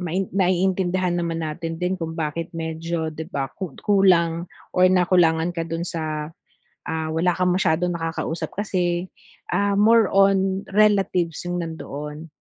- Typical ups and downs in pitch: No, narrow, 2.3 semitones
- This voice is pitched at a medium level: Yes, medium, 175 Hz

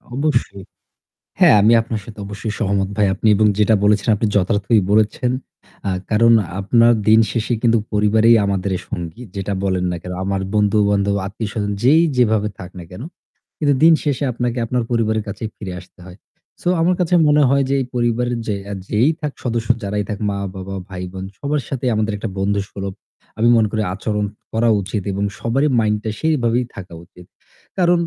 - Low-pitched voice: Yes, low, 110 Hz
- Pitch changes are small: No, average, 3.1 semitones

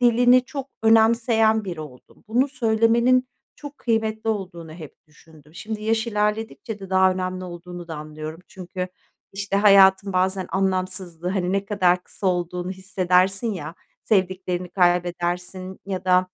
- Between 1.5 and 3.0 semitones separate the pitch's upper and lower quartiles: No, average, 3.7 semitones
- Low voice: No, high, 190 Hz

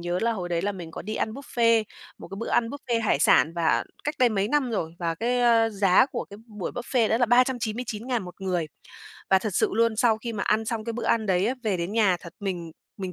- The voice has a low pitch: No, high, 215 Hz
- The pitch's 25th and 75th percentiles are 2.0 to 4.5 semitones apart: Yes, average, 4.1 semitones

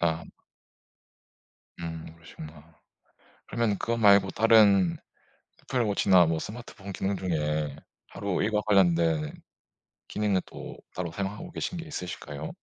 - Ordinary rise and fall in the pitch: Yes, average, 4.3 semitones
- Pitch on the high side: No, very low, 95 Hz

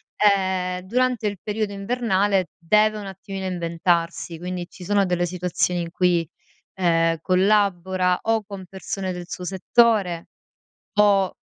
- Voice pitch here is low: No, medium, 185 Hz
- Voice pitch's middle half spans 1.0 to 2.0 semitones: No, narrow, 2.5 semitones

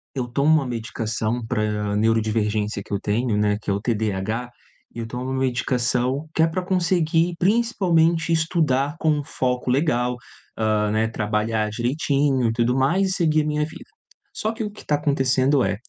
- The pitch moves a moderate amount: No, wide, 6.1 semitones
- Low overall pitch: Yes, low, 125 Hz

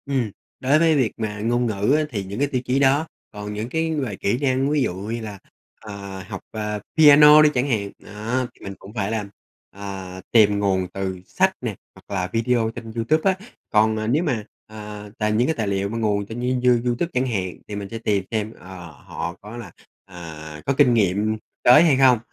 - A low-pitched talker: Yes, low, 110 Hz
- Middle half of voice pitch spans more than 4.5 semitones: No, average, 4.2 semitones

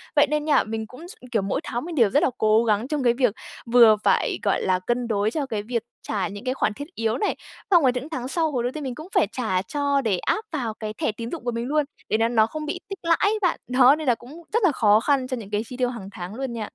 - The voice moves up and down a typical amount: Yes, average, 5.0 semitones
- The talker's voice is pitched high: Yes, high, 245 Hz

